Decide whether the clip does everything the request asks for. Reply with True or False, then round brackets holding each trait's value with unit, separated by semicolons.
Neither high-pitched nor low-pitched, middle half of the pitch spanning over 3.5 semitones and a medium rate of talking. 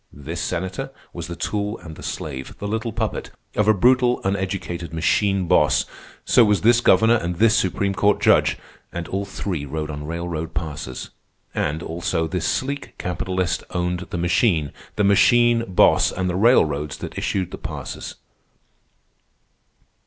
False (90 Hz; 4.0 semitones; 150 wpm)